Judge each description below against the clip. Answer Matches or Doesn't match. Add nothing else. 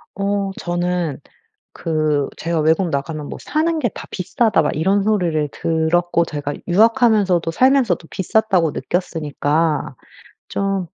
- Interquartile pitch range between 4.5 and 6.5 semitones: Doesn't match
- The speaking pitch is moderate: Matches